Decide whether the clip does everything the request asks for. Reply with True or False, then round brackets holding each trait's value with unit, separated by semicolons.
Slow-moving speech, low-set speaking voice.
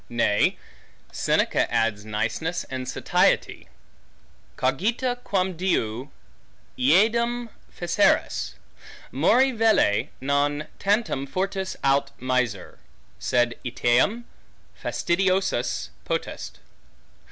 False (75 wpm; 145 Hz)